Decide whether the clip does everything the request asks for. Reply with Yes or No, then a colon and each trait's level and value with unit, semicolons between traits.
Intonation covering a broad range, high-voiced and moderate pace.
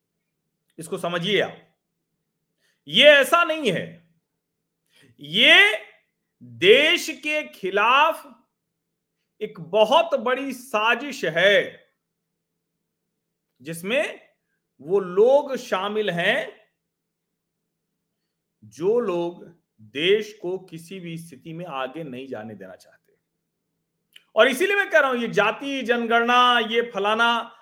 No: wide, 8.5 semitones; high, 215 Hz; slow, 100 wpm